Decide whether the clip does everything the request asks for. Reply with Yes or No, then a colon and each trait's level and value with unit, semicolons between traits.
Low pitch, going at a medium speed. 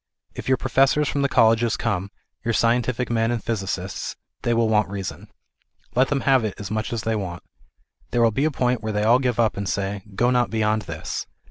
No: low, 115 Hz; fast, 225 wpm